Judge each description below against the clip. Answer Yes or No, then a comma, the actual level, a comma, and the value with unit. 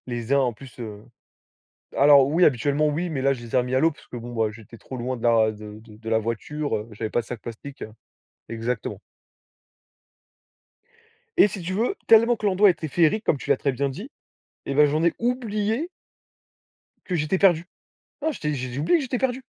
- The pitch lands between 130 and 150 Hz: Yes, medium, 140 Hz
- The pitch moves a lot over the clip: Yes, wide, 7.4 semitones